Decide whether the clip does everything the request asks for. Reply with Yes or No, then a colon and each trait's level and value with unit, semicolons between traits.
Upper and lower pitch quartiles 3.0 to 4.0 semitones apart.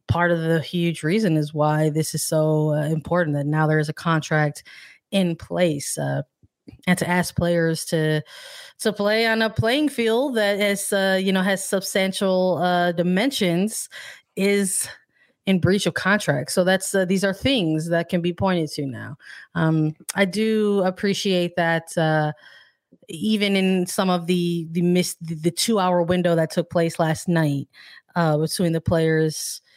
Yes: average, 3.5 semitones